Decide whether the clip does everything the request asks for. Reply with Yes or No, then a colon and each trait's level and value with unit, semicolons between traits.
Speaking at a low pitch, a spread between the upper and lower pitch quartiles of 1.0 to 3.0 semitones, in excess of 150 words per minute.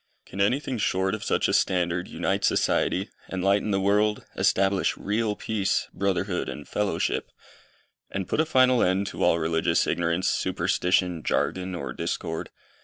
No: very low, 95 Hz; average, 2.7 semitones; average, 145 wpm